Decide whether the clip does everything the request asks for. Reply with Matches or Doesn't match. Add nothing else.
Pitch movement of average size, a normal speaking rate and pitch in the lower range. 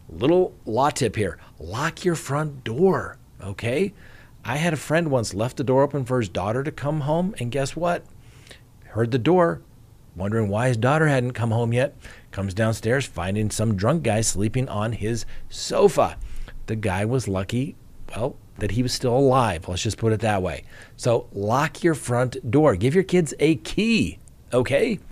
Matches